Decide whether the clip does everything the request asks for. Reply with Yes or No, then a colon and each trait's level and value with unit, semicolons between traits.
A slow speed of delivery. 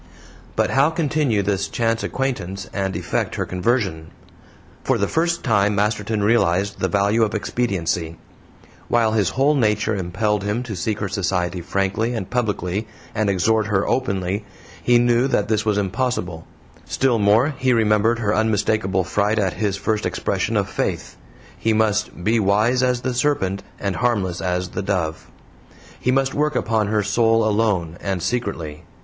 No: average, 160 wpm